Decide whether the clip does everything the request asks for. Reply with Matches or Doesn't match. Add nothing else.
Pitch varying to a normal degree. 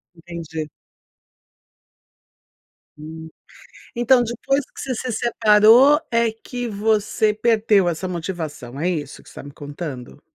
Doesn't match